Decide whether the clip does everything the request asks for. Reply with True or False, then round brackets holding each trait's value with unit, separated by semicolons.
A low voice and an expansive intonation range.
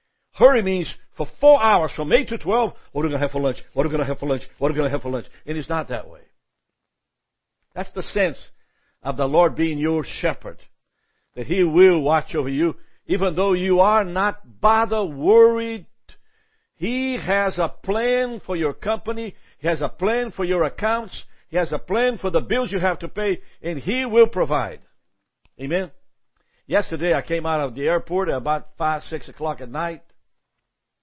False (175 Hz; 6.3 semitones)